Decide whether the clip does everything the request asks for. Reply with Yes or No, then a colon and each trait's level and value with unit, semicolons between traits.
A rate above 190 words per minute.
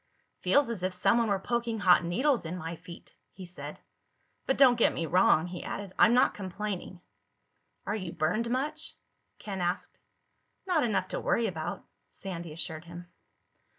No: average, 160 wpm